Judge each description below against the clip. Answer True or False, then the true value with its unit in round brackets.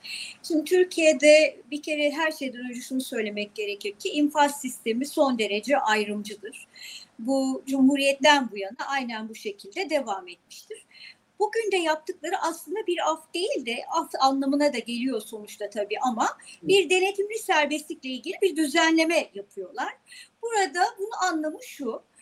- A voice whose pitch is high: True (295 Hz)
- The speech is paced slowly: False (140 wpm)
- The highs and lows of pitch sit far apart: True (6.3 semitones)